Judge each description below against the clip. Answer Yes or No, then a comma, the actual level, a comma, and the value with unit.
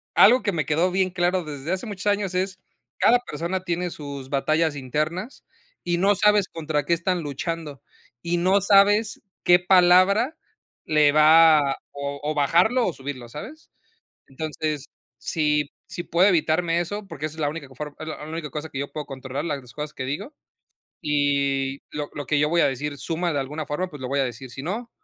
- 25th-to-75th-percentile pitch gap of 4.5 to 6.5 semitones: No, average, 4.1 semitones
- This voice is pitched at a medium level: Yes, medium, 155 Hz